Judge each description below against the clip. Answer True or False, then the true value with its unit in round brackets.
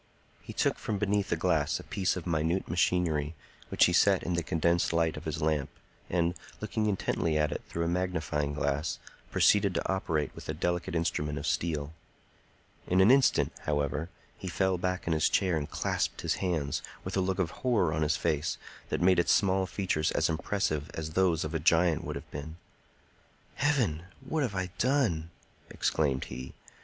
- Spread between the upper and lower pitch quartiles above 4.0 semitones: False (3.4 semitones)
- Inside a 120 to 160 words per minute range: False (185 wpm)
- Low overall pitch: True (85 Hz)